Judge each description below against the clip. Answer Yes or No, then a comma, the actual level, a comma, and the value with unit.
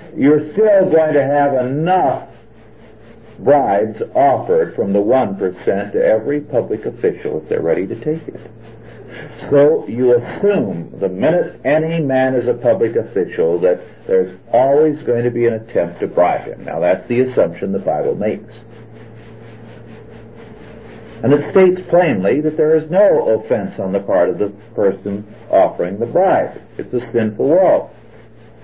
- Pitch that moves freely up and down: Yes, wide, 7.9 semitones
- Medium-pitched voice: No, low, 130 Hz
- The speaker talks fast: No, average, 150 wpm